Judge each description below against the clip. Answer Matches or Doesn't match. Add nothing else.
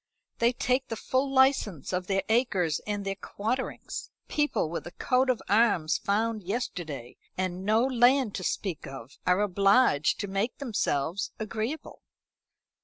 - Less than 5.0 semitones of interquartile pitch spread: Doesn't match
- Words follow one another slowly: Doesn't match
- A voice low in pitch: Doesn't match